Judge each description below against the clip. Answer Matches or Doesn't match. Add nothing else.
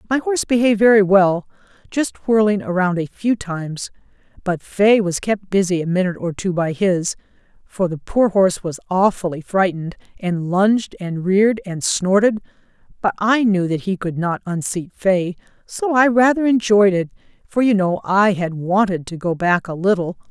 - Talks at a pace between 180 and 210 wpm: Doesn't match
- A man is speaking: Doesn't match